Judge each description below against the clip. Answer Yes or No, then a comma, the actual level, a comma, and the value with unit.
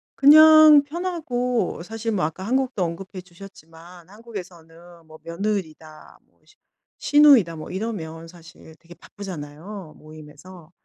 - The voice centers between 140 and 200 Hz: Yes, medium, 185 Hz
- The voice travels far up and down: Yes, wide, 6.1 semitones